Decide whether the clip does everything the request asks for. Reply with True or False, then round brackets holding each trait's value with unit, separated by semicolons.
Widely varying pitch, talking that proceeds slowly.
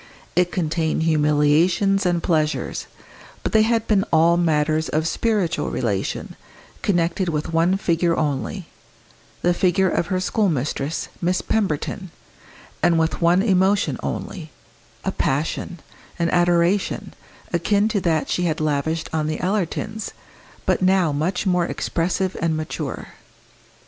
False (3.1 semitones; 130 wpm)